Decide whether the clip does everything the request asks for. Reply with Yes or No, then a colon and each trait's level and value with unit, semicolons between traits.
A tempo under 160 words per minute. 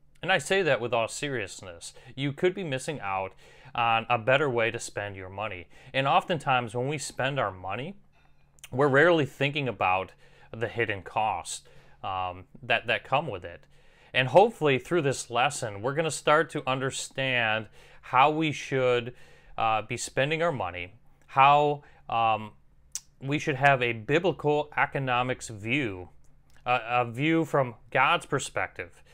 Yes: average, 150 wpm